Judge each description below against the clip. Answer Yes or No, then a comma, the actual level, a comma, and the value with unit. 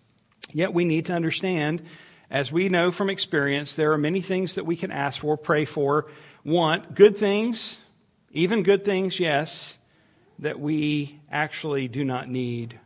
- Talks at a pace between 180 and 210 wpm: No, average, 160 wpm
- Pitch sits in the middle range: Yes, medium, 160 Hz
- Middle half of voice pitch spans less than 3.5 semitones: No, average, 4.2 semitones